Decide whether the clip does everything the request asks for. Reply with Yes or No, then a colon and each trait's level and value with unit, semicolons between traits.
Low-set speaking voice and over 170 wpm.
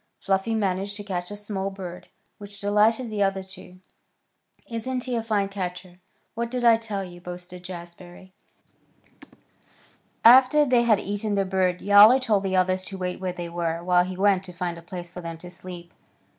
No: high, 195 Hz; average, 185 wpm